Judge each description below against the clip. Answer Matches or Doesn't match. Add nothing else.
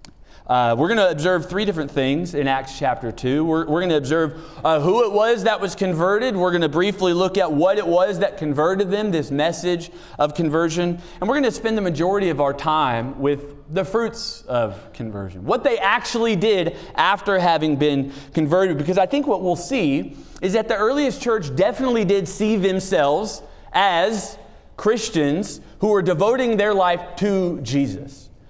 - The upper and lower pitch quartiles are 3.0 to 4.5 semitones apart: Doesn't match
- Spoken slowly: Doesn't match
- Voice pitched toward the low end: Doesn't match